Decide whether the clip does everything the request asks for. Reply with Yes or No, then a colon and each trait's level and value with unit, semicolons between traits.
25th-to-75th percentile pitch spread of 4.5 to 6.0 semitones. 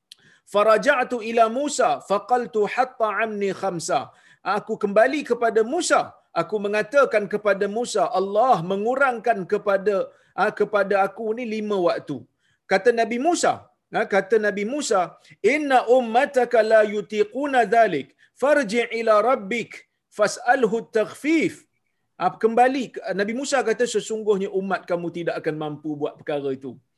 No: average, 3.9 semitones